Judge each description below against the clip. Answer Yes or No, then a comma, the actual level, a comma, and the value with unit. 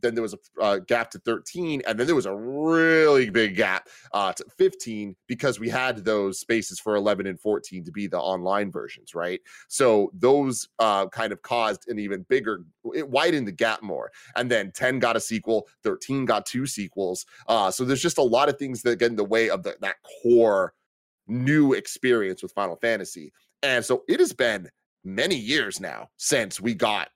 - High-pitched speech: No, low, 120 Hz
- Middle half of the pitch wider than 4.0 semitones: Yes, average, 4.7 semitones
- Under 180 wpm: No, average, 200 wpm